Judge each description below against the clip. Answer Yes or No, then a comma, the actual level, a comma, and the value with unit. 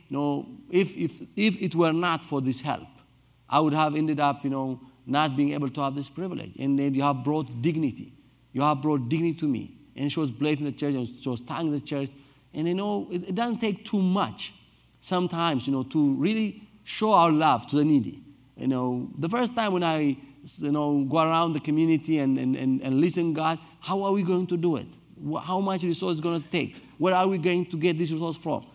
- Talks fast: Yes, fast, 240 wpm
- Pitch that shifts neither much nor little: Yes, average, 3.8 semitones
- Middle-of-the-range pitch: Yes, medium, 155 Hz